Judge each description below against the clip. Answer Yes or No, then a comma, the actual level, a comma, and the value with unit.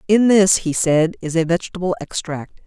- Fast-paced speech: No, average, 180 wpm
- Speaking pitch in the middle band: Yes, medium, 175 Hz